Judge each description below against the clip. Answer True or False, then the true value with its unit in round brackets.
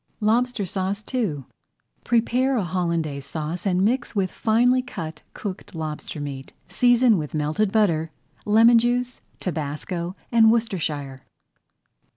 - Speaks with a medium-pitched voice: False (195 Hz)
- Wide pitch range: True (6.8 semitones)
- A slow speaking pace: True (120 wpm)